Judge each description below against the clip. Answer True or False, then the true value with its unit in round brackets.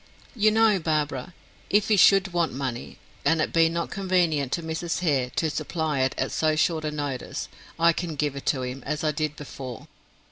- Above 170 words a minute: True (200 wpm)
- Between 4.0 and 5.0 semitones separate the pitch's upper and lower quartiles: False (3.4 semitones)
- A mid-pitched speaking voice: True (155 Hz)